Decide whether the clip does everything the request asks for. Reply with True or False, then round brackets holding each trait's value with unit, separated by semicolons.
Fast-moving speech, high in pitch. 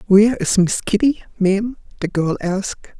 False (160 wpm; 200 Hz)